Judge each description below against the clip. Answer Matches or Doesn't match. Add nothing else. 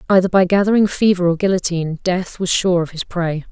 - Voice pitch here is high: Doesn't match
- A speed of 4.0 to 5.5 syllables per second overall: Doesn't match